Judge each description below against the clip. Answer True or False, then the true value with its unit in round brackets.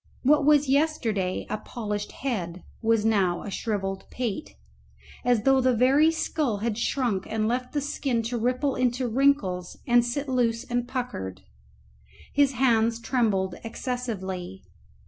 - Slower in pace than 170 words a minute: True (140 wpm)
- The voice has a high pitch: True (240 Hz)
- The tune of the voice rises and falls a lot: False (4.0 semitones)